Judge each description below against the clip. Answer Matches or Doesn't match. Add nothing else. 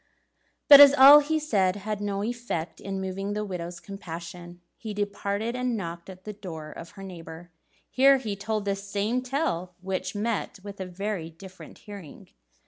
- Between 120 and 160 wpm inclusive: Doesn't match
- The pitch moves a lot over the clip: Doesn't match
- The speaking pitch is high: Matches